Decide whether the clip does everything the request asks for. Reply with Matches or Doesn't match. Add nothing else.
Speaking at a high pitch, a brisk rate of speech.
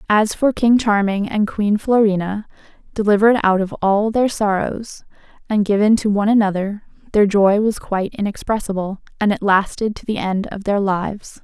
Doesn't match